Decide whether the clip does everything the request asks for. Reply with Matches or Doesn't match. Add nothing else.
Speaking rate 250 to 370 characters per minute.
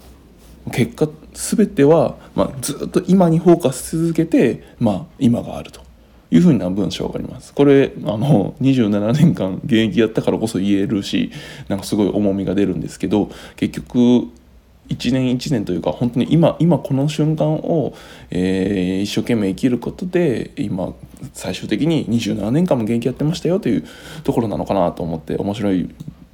Matches